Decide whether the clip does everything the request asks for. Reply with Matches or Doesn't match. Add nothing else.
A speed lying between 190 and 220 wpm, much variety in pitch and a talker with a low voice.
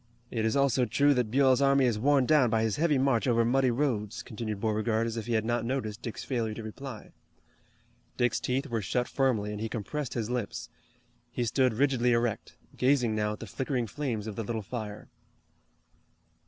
Doesn't match